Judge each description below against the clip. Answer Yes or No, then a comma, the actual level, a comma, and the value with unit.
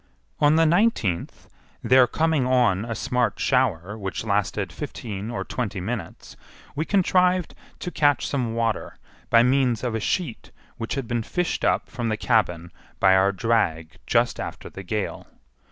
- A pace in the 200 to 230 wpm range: No, average, 155 wpm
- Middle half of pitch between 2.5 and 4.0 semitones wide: No, average, 5.1 semitones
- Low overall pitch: Yes, low, 115 Hz